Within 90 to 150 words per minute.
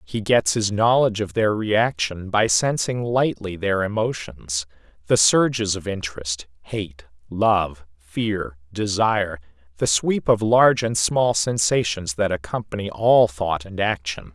Yes: average, 140 wpm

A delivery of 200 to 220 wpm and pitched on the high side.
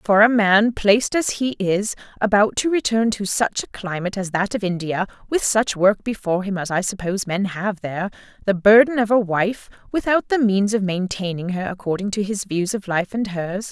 Yes: fast, 205 wpm; high, 205 Hz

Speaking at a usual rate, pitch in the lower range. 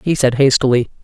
Yes: average, 175 wpm; low, 130 Hz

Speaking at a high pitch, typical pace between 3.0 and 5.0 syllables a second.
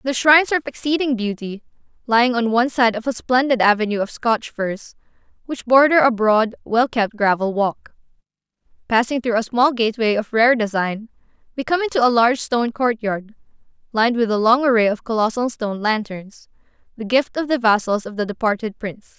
No: high, 230 Hz; 5.6 syllables/s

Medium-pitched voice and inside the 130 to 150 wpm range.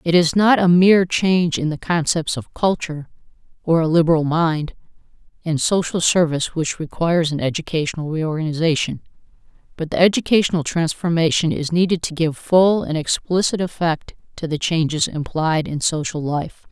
Yes: medium, 165 Hz; average, 145 wpm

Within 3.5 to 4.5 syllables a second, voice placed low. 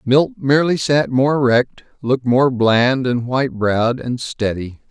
Yes: 4.4 syllables/s; low, 130 Hz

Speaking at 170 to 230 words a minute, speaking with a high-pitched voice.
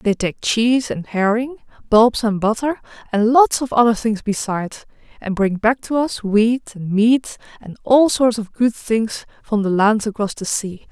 Yes: average, 185 wpm; high, 225 Hz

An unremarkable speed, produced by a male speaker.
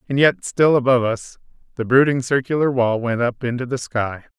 Yes: average, 190 wpm; male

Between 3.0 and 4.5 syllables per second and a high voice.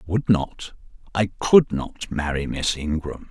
No: 4.1 syllables/s; very low, 90 Hz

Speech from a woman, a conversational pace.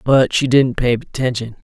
No: male; average, 175 wpm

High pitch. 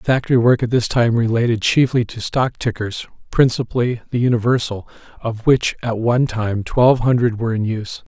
No: low, 120 Hz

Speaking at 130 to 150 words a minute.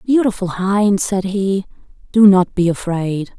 Yes: average, 140 wpm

